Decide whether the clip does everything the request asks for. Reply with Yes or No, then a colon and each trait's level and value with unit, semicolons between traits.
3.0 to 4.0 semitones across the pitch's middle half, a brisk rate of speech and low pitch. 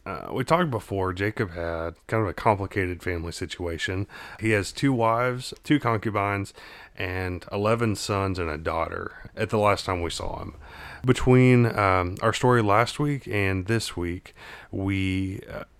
No: average, 3.6 semitones; average, 160 wpm; low, 100 Hz